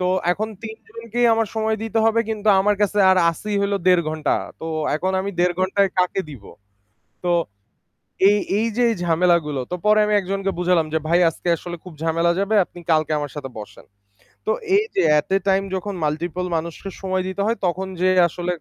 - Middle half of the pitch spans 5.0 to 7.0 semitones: No, average, 3.5 semitones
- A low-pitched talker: No, medium, 185 Hz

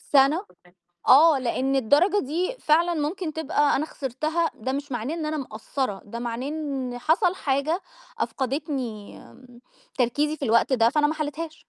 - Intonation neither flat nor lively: Yes, average, 3.5 semitones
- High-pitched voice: Yes, very high, 285 Hz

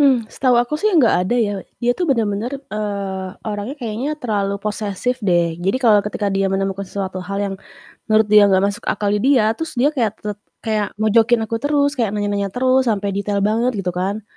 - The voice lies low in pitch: No, high, 215 Hz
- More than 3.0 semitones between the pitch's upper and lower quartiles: Yes, average, 3.6 semitones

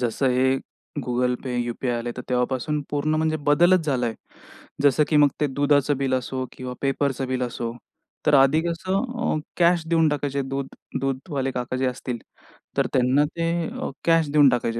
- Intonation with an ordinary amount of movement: Yes, average, 3.2 semitones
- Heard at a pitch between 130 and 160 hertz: Yes, low, 135 Hz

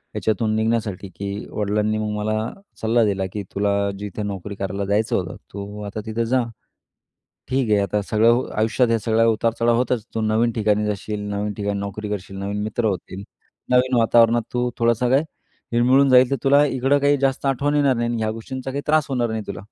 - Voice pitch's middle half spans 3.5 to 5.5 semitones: No, average, 3.1 semitones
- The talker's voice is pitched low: Yes, low, 110 Hz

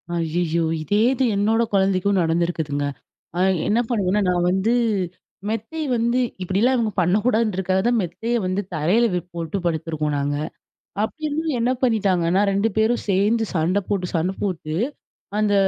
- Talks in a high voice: Yes, high, 195 Hz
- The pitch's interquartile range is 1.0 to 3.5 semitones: No, average, 4.7 semitones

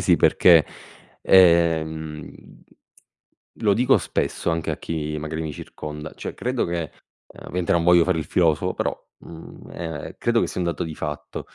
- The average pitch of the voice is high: No, very low, 80 Hz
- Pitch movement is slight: Yes, narrow, 2.0 semitones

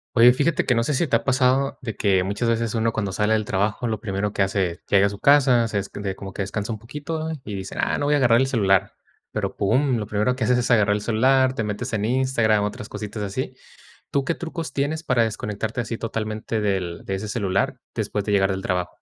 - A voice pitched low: Yes, low, 110 Hz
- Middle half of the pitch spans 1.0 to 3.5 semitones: No, average, 4.0 semitones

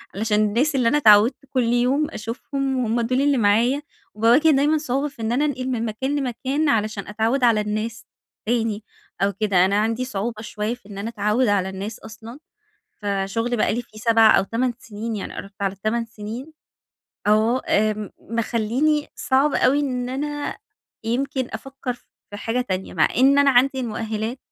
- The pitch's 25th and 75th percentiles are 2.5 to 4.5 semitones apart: Yes, average, 3.5 semitones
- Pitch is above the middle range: Yes, high, 230 Hz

